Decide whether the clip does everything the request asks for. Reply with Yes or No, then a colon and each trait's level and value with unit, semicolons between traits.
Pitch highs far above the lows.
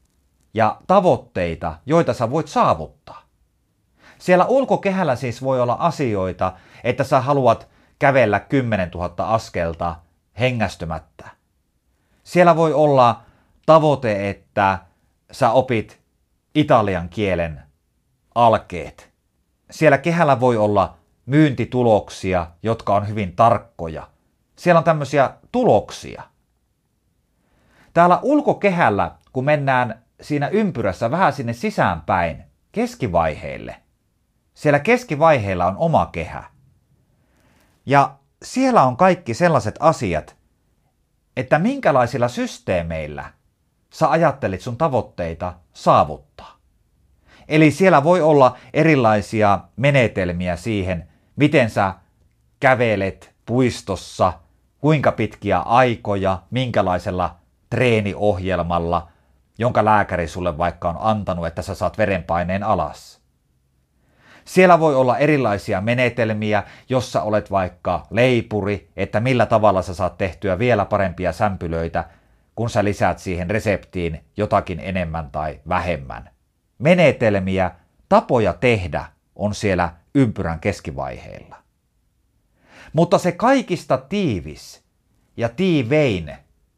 Yes: wide, 7.2 semitones